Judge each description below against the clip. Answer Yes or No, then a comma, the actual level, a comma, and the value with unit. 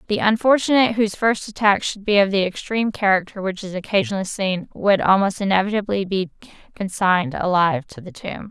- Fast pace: No, average, 170 wpm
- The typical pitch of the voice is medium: No, high, 200 Hz